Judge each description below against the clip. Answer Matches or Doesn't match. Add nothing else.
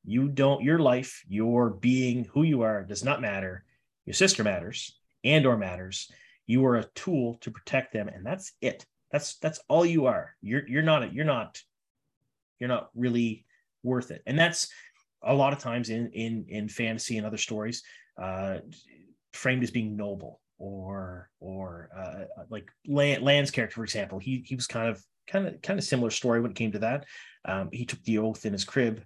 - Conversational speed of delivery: Matches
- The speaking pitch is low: Matches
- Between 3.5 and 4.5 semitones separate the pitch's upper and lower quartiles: Matches